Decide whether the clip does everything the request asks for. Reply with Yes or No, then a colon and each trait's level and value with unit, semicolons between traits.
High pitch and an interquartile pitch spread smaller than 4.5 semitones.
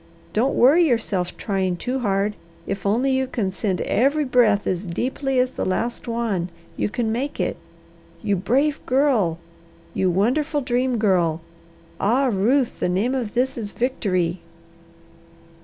No: high, 230 Hz; average, 5.1 semitones